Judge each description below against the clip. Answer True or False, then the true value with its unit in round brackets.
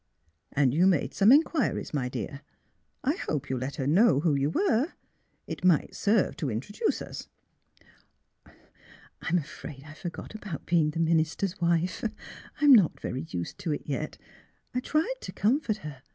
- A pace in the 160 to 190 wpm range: True (170 wpm)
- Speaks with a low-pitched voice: False (170 Hz)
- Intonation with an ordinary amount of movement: False (6.8 semitones)